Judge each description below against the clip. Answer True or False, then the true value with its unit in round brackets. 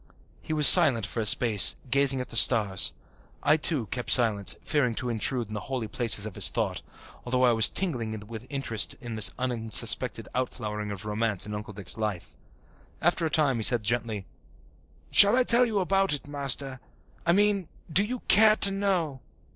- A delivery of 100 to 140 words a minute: False (185 wpm)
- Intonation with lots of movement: True (6.1 semitones)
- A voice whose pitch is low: True (125 Hz)